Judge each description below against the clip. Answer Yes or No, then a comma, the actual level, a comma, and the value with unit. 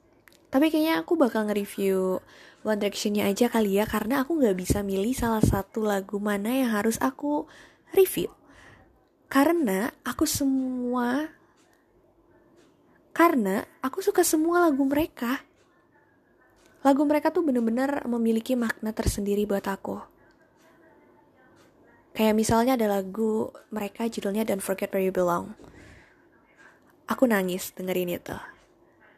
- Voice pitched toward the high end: Yes, high, 240 Hz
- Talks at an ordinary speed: Yes, average, 115 wpm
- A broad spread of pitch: Yes, wide, 6.8 semitones